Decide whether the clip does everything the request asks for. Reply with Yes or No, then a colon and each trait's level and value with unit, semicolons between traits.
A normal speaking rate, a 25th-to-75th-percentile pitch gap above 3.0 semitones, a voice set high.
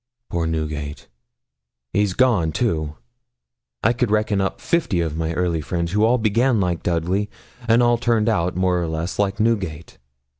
No: average, 160 wpm; average, 5.1 semitones; very low, 95 Hz